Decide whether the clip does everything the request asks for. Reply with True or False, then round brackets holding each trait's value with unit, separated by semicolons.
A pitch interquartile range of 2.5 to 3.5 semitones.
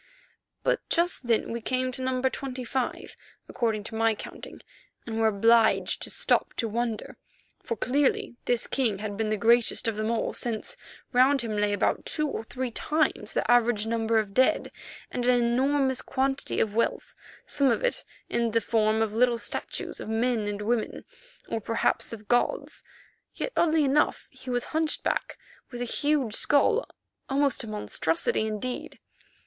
True (2.9 semitones)